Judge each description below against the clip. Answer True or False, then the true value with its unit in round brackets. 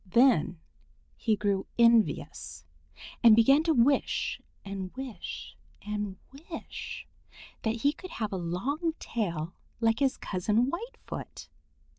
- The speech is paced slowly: True (115 wpm)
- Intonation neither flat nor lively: False (5.9 semitones)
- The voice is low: False (225 Hz)